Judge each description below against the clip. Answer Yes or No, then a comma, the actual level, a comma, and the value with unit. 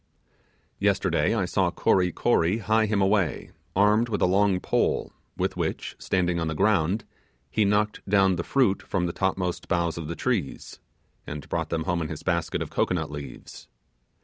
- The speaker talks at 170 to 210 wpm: Yes, average, 175 wpm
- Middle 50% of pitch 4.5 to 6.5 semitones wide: No, average, 3.5 semitones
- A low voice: Yes, very low, 95 Hz